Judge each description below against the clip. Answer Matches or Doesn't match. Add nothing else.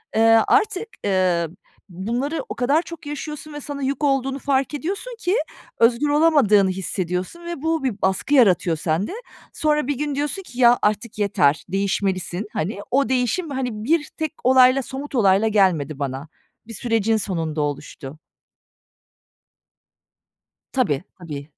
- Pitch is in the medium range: Doesn't match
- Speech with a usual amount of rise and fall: Doesn't match